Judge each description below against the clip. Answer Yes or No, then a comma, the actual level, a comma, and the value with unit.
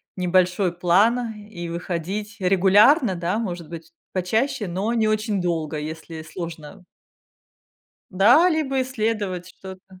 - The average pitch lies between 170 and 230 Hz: Yes, high, 190 Hz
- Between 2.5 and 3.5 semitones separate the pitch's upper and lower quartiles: No, average, 4.0 semitones